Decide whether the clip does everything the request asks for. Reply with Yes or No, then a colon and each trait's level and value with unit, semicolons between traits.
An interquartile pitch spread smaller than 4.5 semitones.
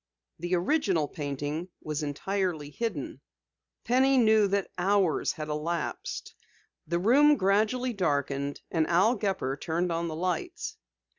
No: average, 5.1 semitones